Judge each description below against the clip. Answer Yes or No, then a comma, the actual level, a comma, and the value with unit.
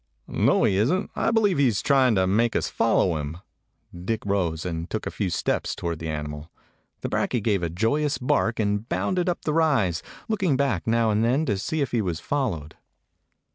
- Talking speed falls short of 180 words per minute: No, fast, 205 wpm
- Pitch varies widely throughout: Yes, wide, 7.9 semitones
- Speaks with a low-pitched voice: Yes, low, 110 Hz